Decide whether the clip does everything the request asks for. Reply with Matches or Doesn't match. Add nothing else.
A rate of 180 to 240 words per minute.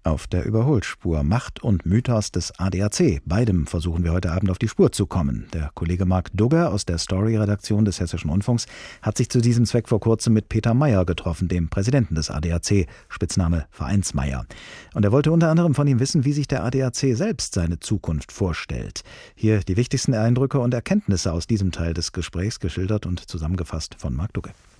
Matches